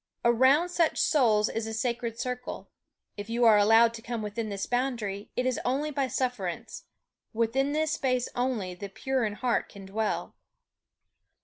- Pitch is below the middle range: No, high, 235 Hz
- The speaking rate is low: No, average, 165 wpm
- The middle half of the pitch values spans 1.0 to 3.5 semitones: Yes, average, 3.2 semitones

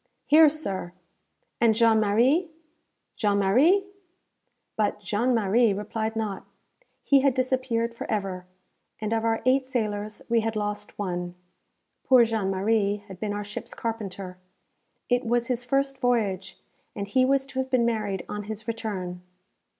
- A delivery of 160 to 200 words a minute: No, average, 150 wpm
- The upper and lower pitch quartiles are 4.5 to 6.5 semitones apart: No, average, 3.4 semitones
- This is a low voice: No, high, 220 Hz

